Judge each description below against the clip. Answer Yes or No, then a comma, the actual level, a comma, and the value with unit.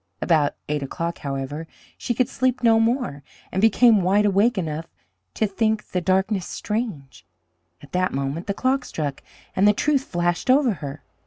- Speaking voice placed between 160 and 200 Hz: Yes, high, 190 Hz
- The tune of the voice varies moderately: No, wide, 6.6 semitones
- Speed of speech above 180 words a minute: No, average, 165 wpm